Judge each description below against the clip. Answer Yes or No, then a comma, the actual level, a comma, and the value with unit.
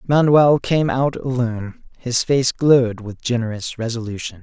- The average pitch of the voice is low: Yes, low, 125 Hz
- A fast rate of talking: No, slow, 135 wpm